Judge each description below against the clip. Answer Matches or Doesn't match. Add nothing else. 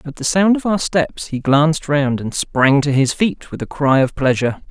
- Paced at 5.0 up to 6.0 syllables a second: Doesn't match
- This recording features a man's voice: Matches